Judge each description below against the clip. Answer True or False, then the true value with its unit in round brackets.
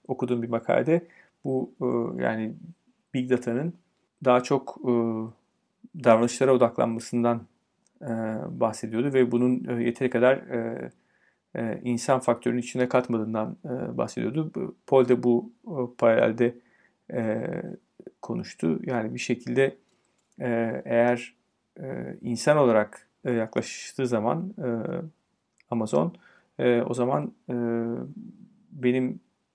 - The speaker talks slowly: True (75 wpm)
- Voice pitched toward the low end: True (125 Hz)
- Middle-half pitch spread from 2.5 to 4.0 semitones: True (2.8 semitones)